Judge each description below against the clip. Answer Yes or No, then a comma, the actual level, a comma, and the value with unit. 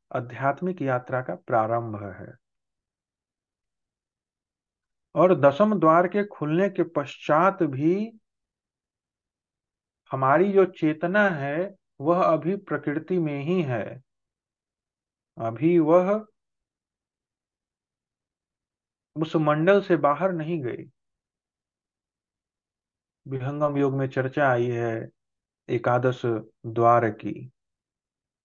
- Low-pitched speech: No, medium, 150 Hz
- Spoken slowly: Yes, slow, 85 wpm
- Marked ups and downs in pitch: Yes, wide, 6.0 semitones